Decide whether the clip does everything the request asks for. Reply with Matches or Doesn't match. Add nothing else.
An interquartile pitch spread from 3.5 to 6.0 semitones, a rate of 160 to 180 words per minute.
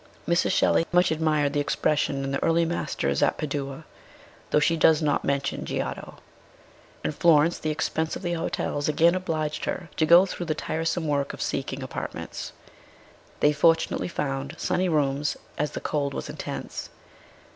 Doesn't match